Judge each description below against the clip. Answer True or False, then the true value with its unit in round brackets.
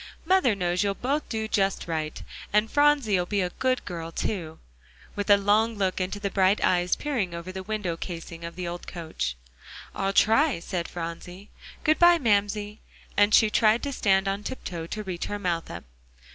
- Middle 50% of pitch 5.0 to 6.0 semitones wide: False (3.7 semitones)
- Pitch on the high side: True (195 Hz)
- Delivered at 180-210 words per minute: True (185 wpm)